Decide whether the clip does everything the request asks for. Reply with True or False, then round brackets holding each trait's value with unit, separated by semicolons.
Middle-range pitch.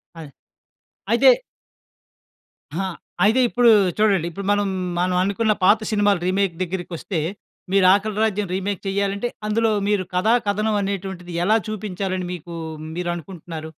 False (195 Hz)